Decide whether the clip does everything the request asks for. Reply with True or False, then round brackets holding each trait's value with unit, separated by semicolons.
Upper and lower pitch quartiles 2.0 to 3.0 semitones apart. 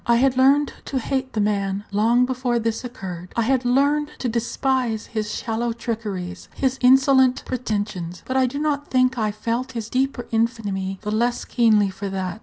False (3.7 semitones)